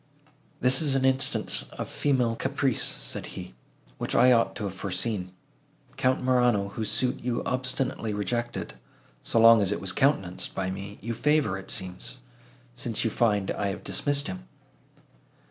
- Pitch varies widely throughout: No, average, 4.5 semitones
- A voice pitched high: No, low, 115 Hz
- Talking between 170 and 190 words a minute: No, average, 160 wpm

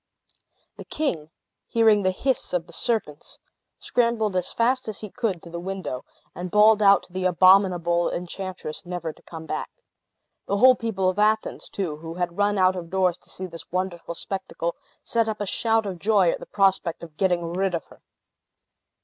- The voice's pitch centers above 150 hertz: Yes, medium, 185 Hz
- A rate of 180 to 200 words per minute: Yes, average, 185 wpm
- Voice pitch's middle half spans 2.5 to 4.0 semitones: Yes, average, 3.4 semitones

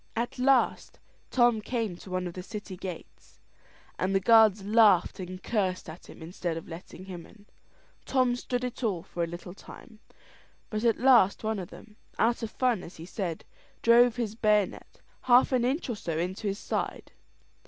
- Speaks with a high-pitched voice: Yes, high, 210 Hz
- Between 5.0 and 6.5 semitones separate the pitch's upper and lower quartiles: No, average, 4.4 semitones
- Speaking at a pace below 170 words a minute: No, average, 185 wpm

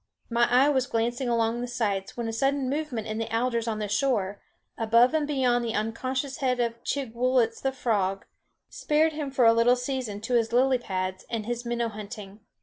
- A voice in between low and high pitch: No, high, 240 Hz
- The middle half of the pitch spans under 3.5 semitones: Yes, narrow, 2.5 semitones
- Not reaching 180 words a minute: No, average, 195 wpm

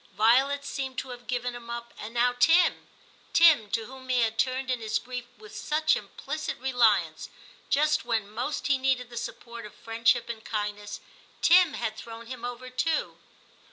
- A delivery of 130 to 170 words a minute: No, average, 185 wpm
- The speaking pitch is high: Yes, high, 245 Hz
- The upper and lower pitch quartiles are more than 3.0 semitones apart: No, narrow, 2.5 semitones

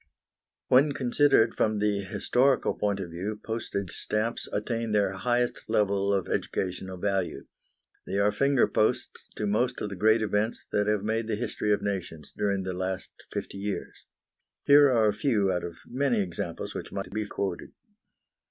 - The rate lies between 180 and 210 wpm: No, average, 165 wpm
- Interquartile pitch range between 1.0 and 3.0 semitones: Yes, average, 2.7 semitones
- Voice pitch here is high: No, low, 105 Hz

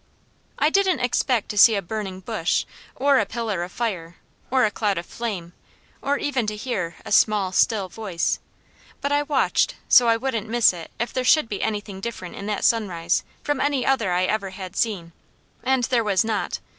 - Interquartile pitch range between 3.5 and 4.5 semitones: No, average, 4.9 semitones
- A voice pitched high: Yes, high, 215 Hz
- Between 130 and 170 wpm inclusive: No, average, 195 wpm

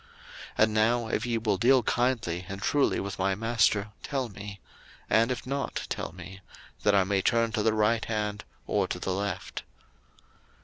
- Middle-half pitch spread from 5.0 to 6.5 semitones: No, average, 2.9 semitones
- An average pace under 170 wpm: No, average, 180 wpm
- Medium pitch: No, low, 110 Hz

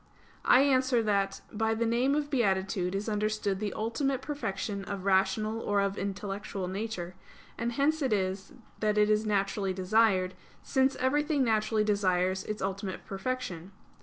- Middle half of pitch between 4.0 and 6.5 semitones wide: No, average, 3.2 semitones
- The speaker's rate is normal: Yes, average, 150 wpm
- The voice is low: No, high, 210 Hz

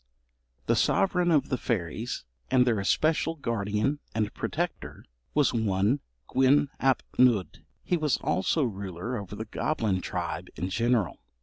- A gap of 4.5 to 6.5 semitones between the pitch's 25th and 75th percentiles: Yes, wide, 5.6 semitones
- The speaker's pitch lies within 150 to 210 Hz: No, low, 115 Hz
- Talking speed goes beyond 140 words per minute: No, slow, 135 wpm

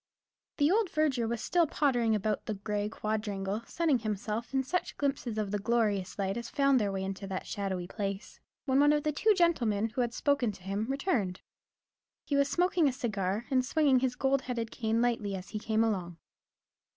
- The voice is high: Yes, high, 230 Hz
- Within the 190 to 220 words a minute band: Yes, average, 195 wpm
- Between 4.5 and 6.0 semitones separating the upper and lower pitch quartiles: Yes, average, 5.2 semitones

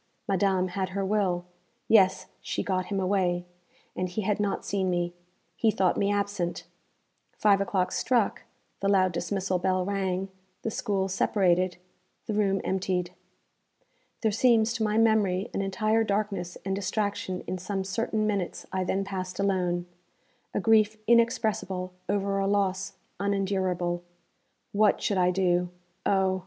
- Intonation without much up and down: Yes, narrow, 1.8 semitones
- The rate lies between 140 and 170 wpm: Yes, average, 145 wpm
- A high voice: Yes, high, 195 Hz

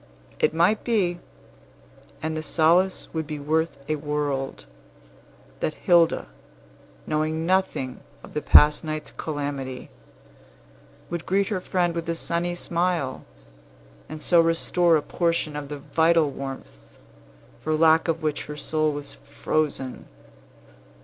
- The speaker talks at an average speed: No, slow, 130 wpm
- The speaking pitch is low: No, medium, 160 Hz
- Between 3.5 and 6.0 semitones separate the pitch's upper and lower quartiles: No, narrow, 2.4 semitones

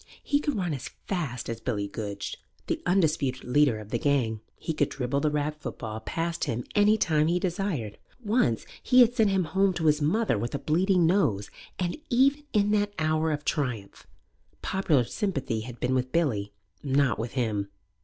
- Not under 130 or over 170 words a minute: No, average, 185 wpm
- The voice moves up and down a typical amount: No, wide, 7.8 semitones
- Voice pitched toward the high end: No, medium, 150 Hz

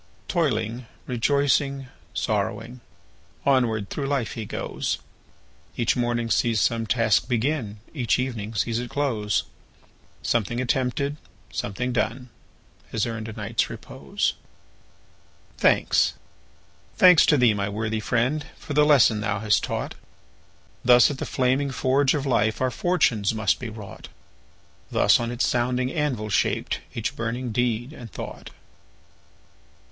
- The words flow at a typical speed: No, slow, 125 wpm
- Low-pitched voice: Yes, low, 120 Hz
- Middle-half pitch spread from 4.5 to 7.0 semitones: No, average, 3.1 semitones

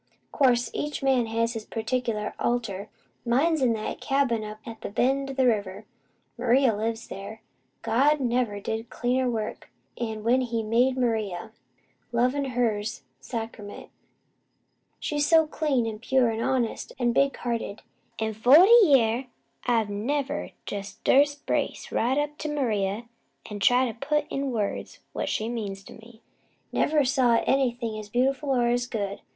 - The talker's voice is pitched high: Yes, high, 240 Hz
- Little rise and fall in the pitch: No, average, 3.2 semitones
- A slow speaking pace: No, average, 155 wpm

